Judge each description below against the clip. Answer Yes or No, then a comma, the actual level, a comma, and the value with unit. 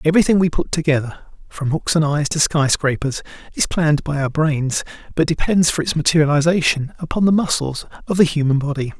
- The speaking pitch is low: No, medium, 155 Hz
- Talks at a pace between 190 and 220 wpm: No, average, 165 wpm